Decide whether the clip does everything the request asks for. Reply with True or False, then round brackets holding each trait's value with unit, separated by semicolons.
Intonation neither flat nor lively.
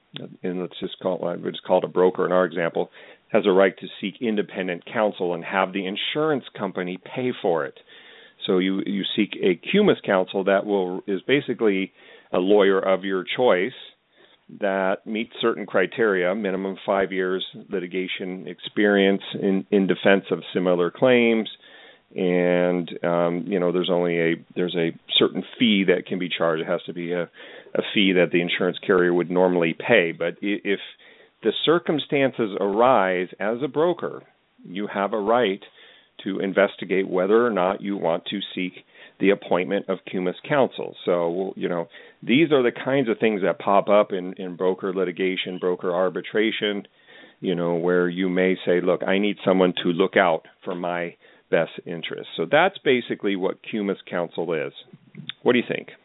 False (2.0 semitones)